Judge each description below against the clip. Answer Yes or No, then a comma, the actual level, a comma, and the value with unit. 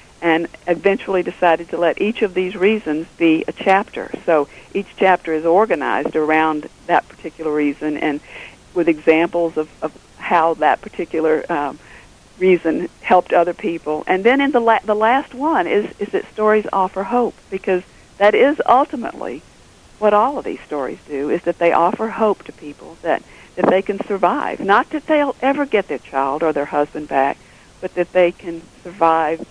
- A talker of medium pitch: Yes, medium, 175 Hz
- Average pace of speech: Yes, average, 175 wpm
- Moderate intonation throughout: Yes, average, 4.5 semitones